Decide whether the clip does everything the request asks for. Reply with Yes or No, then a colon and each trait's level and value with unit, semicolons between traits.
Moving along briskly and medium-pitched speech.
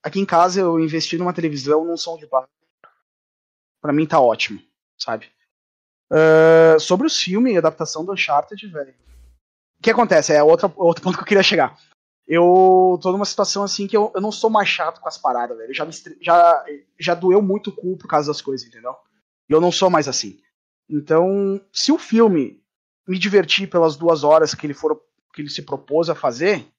Yes: fast, 195 wpm; medium, 170 Hz